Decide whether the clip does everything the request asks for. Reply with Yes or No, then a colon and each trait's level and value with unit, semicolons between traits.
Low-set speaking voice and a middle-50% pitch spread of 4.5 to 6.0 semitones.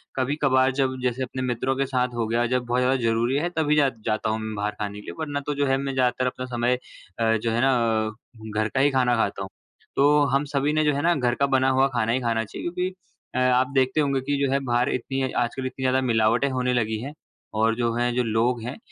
No: low, 125 Hz; narrow, 2.5 semitones